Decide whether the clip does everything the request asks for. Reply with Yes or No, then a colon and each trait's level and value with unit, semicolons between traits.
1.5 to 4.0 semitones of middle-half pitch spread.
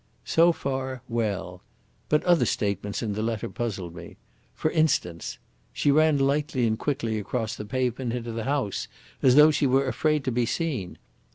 No: average, 4.8 semitones